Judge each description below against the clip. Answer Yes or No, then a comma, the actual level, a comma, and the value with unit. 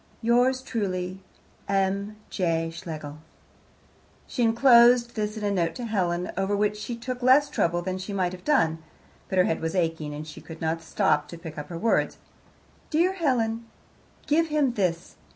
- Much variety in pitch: Yes, wide, 5.9 semitones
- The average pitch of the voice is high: Yes, high, 195 Hz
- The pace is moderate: Yes, average, 170 wpm